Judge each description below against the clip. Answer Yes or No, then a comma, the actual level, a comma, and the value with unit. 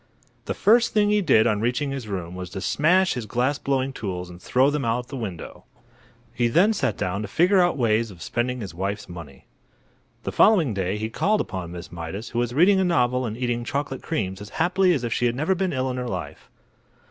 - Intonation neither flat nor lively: No, wide, 6.8 semitones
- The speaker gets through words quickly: Yes, fast, 230 wpm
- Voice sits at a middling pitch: No, low, 120 Hz